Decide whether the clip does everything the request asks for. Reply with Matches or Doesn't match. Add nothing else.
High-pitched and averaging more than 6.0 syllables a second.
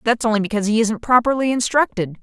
Matches